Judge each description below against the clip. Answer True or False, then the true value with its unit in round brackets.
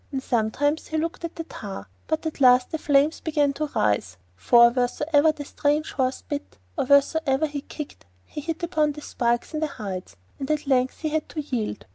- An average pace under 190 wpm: False (200 wpm)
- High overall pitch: True (290 Hz)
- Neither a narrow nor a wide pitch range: True (3.7 semitones)